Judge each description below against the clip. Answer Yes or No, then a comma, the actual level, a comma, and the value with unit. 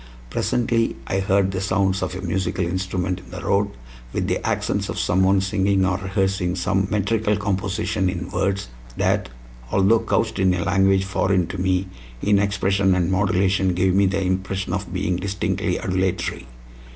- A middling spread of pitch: No, narrow, 1.1 semitones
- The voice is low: Yes, very low, 95 Hz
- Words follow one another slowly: No, average, 165 wpm